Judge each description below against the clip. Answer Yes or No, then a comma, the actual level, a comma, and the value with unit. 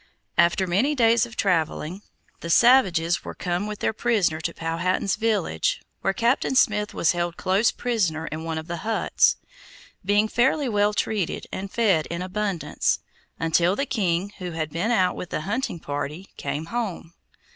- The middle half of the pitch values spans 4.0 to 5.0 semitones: Yes, average, 4.6 semitones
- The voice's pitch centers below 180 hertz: No, high, 190 Hz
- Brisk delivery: No, average, 165 wpm